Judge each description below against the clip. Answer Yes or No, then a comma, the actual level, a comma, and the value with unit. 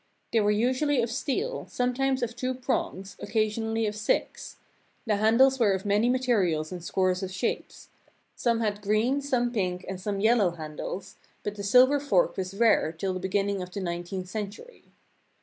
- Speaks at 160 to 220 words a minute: Yes, average, 170 wpm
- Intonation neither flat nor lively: Yes, average, 4.4 semitones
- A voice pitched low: No, high, 210 Hz